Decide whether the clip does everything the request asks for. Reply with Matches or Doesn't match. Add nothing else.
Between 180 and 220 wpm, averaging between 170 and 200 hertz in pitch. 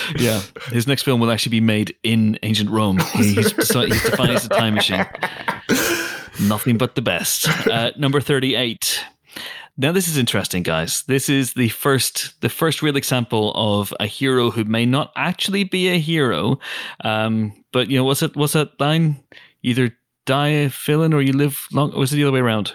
Doesn't match